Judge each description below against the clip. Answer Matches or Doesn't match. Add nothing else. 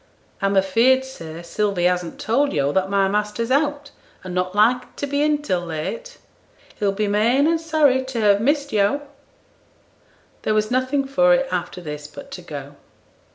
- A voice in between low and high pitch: Doesn't match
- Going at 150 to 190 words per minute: Matches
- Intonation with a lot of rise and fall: Matches